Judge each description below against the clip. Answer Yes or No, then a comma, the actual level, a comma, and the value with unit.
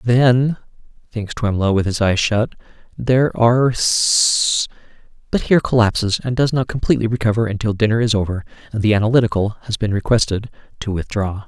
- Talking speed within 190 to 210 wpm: No, average, 155 wpm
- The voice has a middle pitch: No, low, 110 Hz